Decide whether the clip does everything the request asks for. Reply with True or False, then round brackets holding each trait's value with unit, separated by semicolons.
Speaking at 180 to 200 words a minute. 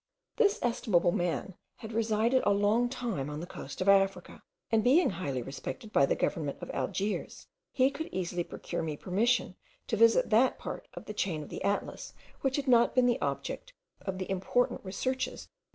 True (190 wpm)